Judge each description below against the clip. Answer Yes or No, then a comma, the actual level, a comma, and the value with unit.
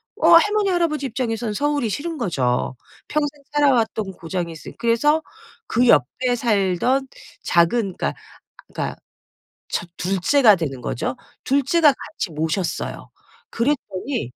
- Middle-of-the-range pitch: No, high, 235 Hz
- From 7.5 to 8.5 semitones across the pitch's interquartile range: Yes, wide, 8.2 semitones